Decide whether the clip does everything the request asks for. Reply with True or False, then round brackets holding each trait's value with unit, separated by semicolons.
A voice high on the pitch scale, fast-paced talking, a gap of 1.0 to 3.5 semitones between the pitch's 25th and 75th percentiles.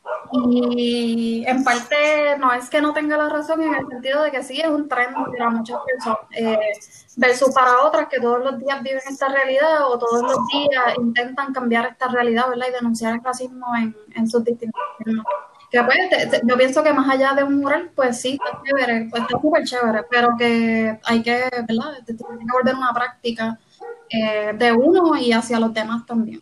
True (250 Hz; 200 wpm; 2.8 semitones)